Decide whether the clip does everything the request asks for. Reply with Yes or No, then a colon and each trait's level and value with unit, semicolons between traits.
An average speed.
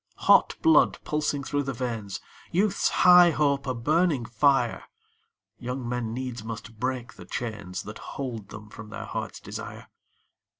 Yes: average, 145 wpm